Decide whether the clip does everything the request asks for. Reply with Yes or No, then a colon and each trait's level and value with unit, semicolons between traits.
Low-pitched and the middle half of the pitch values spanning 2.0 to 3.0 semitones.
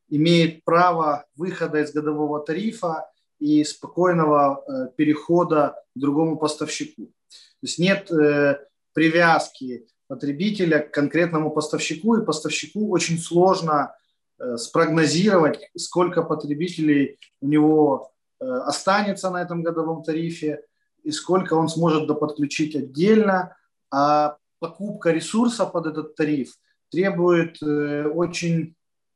No: medium, 160 Hz; average, 2.7 semitones